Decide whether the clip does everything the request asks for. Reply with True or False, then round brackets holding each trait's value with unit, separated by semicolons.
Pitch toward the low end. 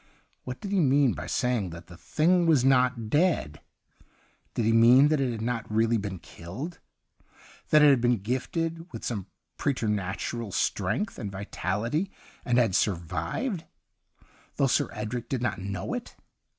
True (120 Hz)